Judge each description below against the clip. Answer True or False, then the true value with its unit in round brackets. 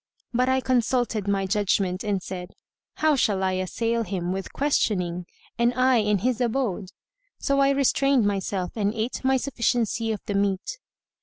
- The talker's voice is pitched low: False (220 Hz)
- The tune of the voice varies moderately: True (4.8 semitones)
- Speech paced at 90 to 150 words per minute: False (160 wpm)